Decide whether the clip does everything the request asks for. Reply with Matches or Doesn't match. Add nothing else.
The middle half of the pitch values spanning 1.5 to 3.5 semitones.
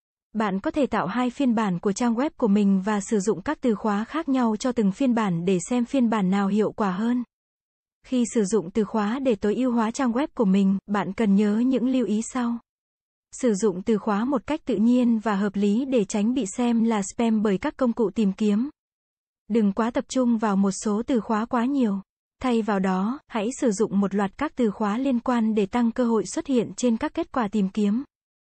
Matches